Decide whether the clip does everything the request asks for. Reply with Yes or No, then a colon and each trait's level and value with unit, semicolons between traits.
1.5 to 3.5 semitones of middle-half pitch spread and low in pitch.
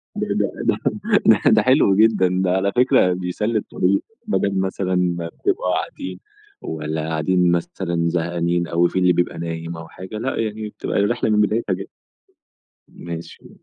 Yes: average, 3.1 semitones; very low, 90 Hz